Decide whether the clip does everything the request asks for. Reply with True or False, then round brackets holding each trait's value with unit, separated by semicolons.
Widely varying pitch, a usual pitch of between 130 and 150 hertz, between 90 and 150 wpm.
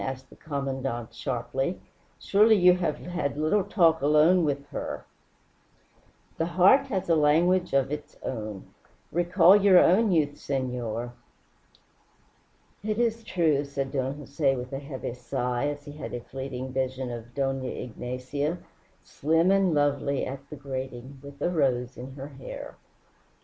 False (4.5 semitones; 140 Hz; 145 wpm)